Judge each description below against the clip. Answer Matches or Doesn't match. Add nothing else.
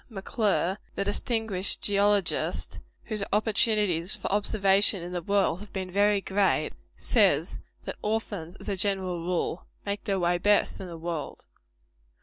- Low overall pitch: Doesn't match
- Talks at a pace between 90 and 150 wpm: Matches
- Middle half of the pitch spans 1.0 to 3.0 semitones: Matches